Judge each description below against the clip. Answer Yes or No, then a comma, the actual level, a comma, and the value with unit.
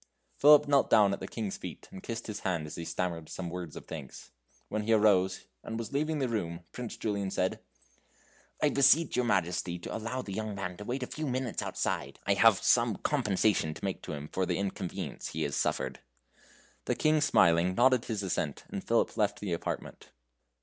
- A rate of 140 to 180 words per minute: No, average, 200 wpm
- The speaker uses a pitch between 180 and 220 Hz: No, low, 100 Hz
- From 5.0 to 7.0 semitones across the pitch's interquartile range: Yes, average, 5.3 semitones